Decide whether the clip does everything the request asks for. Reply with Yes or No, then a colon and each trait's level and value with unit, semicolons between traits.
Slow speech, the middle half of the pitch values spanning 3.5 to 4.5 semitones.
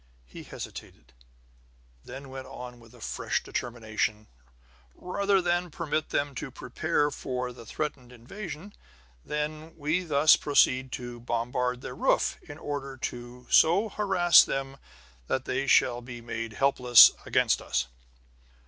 Yes: slow, 130 wpm; average, 4.1 semitones